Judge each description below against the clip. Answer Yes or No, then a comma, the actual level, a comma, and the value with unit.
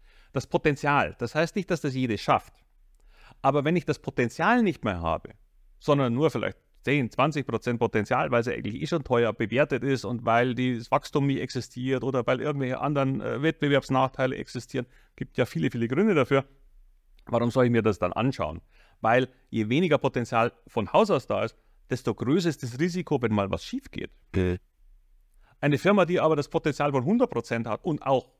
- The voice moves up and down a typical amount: Yes, average, 3.9 semitones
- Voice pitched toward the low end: Yes, low, 130 Hz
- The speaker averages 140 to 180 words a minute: No, fast, 190 wpm